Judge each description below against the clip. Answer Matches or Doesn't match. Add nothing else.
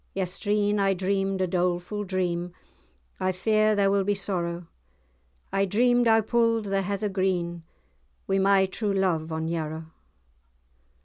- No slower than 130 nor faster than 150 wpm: Matches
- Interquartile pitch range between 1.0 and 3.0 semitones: Matches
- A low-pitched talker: Doesn't match